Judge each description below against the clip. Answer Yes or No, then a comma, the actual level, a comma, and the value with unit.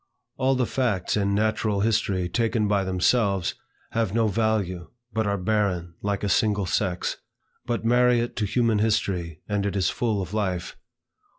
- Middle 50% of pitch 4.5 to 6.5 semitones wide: No, average, 3.1 semitones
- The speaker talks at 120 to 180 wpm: Yes, average, 165 wpm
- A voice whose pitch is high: No, low, 105 Hz